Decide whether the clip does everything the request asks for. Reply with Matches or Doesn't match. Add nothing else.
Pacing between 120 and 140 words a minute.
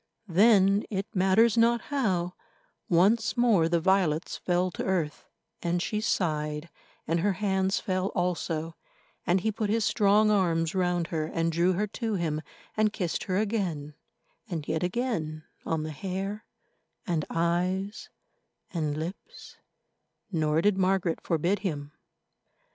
Matches